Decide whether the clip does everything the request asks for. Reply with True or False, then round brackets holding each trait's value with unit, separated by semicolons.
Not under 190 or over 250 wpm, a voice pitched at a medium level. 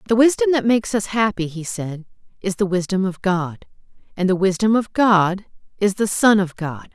False (200 wpm; 195 Hz)